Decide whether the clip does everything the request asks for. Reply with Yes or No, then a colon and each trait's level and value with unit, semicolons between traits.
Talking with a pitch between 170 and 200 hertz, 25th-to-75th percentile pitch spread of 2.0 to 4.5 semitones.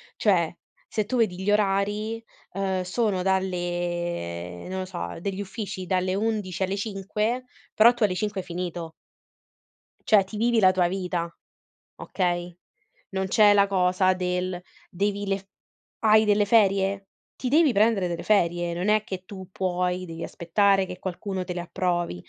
Yes: high, 190 Hz; narrow, 2.5 semitones